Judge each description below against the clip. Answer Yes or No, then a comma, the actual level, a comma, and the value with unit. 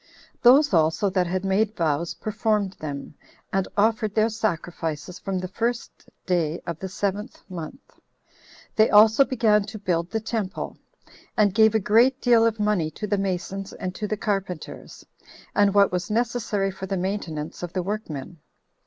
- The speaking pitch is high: Yes, high, 200 Hz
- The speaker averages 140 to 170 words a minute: Yes, average, 160 wpm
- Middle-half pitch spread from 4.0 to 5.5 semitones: No, average, 3.4 semitones